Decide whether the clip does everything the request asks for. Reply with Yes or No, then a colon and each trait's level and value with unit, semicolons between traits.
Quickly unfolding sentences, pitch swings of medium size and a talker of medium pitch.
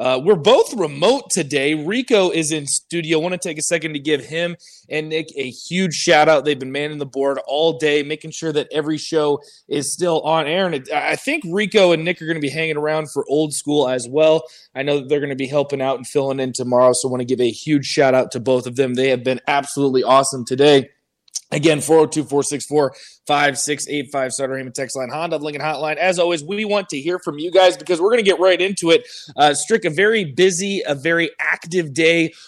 Yes: fast, 230 wpm; average, 3.3 semitones; medium, 155 Hz